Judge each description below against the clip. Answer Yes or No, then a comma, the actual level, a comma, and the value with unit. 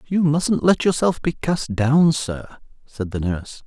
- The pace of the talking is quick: No, average, 180 wpm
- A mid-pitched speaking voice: Yes, medium, 145 Hz